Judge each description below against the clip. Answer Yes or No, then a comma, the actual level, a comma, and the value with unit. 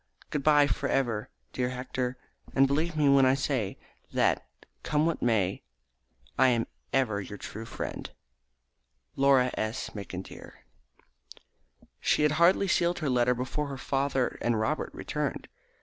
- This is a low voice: Yes, low, 130 Hz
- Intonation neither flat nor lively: Yes, average, 3.5 semitones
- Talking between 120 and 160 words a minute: Yes, average, 140 wpm